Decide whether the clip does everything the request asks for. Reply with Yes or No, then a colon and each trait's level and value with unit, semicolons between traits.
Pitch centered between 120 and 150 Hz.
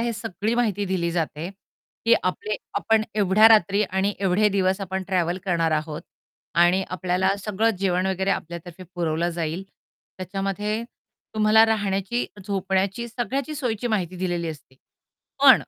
No: high, 190 Hz